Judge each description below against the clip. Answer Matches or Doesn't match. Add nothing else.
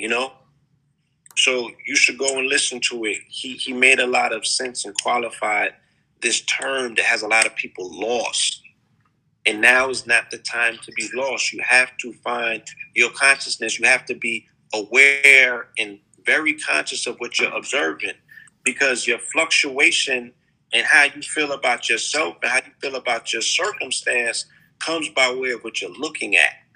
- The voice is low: Matches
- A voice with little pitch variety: Doesn't match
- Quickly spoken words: Doesn't match